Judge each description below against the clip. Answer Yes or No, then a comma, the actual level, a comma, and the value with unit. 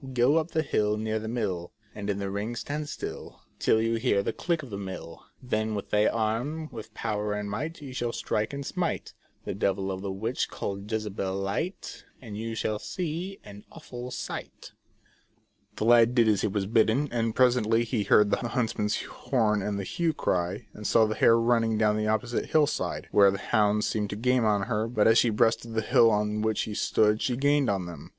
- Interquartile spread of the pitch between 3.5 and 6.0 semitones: No, average, 2.8 semitones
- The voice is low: Yes, low, 110 Hz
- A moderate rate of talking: No, fast, 215 wpm